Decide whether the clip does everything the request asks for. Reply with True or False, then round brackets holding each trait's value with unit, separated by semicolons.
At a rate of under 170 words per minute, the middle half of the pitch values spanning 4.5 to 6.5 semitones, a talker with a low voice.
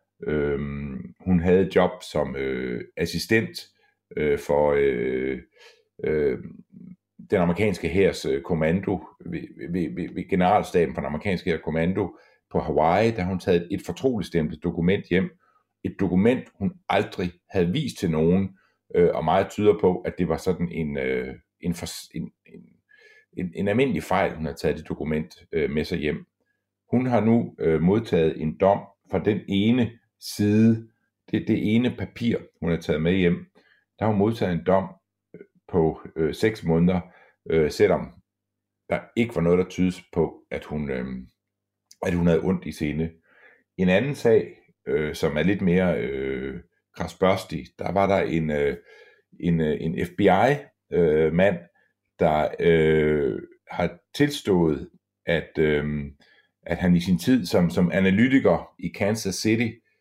True (150 wpm; 5.5 semitones; 90 Hz)